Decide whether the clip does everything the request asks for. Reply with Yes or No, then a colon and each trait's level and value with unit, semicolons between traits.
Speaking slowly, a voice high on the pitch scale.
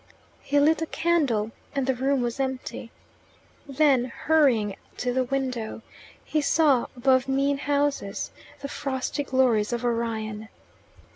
Yes: slow, 130 wpm; very high, 260 Hz